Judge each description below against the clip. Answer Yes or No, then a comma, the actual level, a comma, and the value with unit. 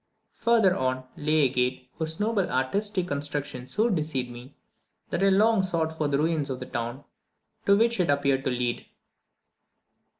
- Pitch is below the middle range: No, medium, 150 Hz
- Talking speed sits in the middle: Yes, average, 165 wpm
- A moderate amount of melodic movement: No, wide, 6.6 semitones